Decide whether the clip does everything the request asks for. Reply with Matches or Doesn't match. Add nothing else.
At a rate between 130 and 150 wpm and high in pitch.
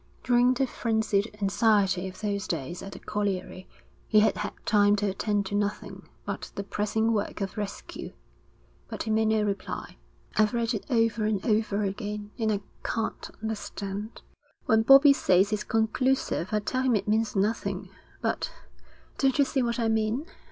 Doesn't match